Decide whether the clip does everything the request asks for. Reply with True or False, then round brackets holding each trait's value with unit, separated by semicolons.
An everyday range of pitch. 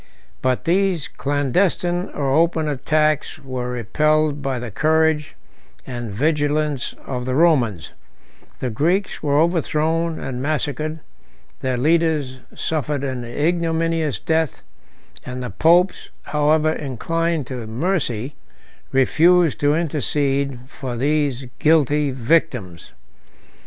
True (3.8 semitones)